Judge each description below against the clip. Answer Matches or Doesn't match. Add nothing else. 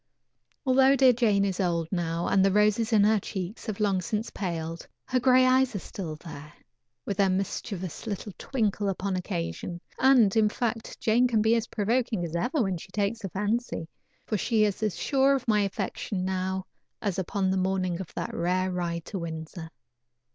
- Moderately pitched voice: Doesn't match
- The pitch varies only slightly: Doesn't match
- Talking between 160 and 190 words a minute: Matches